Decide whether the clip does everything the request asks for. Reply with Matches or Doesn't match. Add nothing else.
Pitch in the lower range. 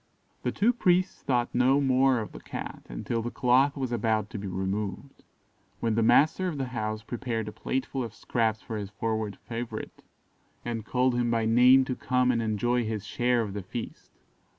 Matches